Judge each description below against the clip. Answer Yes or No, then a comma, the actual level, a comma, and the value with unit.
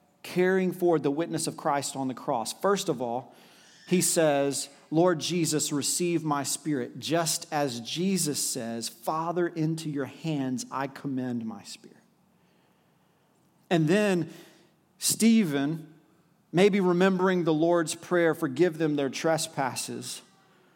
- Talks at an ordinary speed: No, slow, 125 wpm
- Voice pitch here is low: No, medium, 160 Hz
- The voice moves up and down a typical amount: Yes, average, 3.8 semitones